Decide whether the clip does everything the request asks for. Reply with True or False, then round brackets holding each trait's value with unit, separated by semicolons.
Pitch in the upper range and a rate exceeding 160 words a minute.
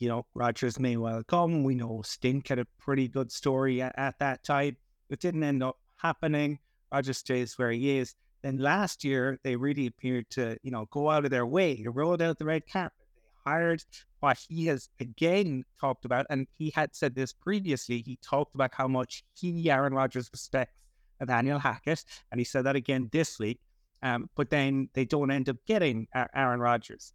False (135 Hz; 200 wpm)